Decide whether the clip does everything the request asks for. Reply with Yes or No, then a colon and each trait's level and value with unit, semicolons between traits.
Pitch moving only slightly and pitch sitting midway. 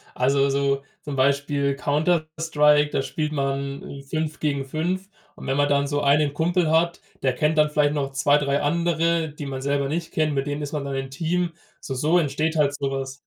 Yes: narrow, 2.2 semitones; medium, 145 Hz